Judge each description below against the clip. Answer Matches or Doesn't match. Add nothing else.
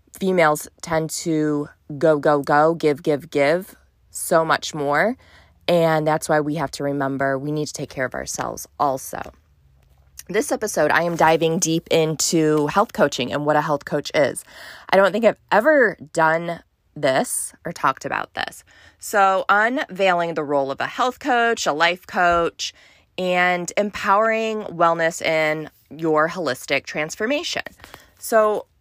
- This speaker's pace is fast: Doesn't match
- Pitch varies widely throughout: Doesn't match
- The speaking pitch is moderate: Matches